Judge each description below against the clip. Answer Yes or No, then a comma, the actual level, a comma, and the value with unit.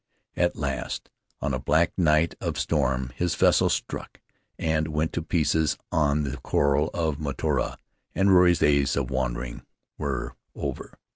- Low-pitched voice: Yes, very low, 75 Hz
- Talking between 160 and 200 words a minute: No, average, 145 wpm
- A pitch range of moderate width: Yes, average, 3.0 semitones